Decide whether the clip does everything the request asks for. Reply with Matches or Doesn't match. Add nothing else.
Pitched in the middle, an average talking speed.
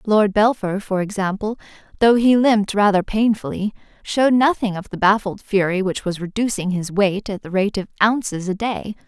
Doesn't match